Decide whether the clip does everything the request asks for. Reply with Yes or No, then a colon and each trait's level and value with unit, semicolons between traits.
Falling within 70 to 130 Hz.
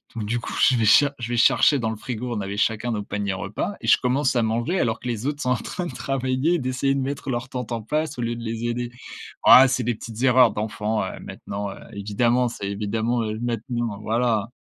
Yes: low, 120 Hz